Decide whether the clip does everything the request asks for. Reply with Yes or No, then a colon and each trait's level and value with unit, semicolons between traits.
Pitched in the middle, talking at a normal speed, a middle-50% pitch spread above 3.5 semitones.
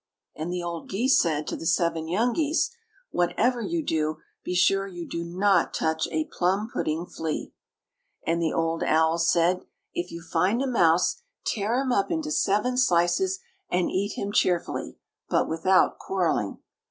Yes: medium, 180 Hz; average, 165 wpm; average, 4.5 semitones